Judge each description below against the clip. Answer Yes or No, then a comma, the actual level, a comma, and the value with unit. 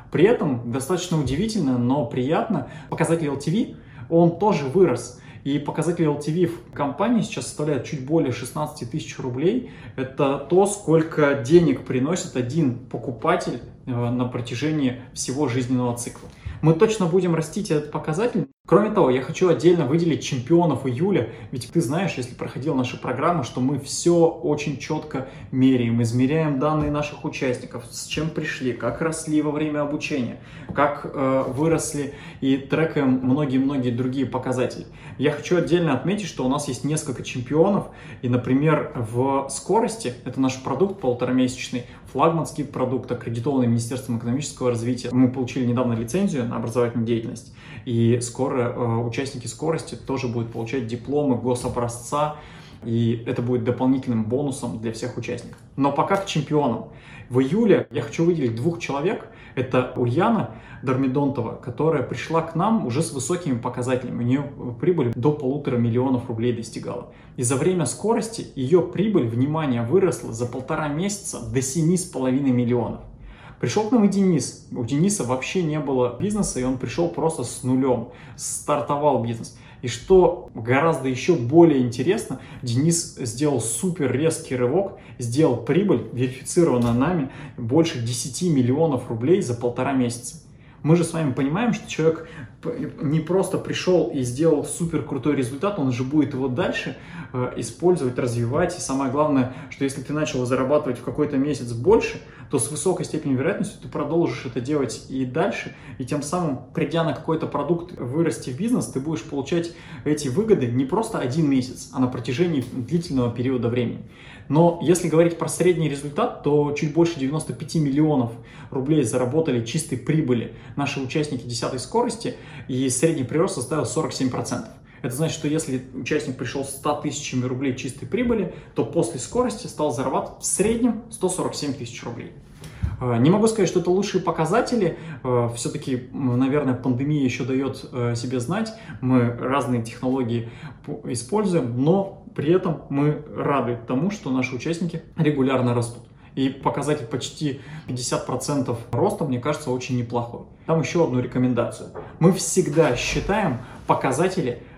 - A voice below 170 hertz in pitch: Yes, medium, 140 Hz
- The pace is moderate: Yes, average, 145 wpm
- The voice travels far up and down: No, average, 4.3 semitones